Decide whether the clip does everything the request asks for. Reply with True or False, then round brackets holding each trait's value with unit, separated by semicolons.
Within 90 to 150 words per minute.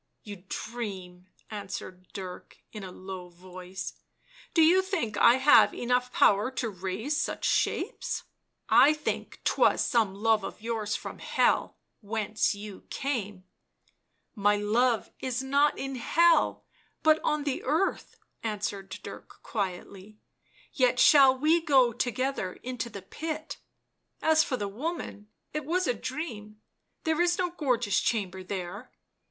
False (160 wpm)